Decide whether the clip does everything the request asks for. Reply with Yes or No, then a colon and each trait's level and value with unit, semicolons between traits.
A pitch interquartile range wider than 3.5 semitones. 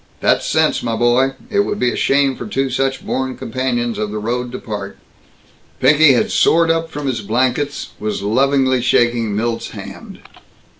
No: average, 2.7 semitones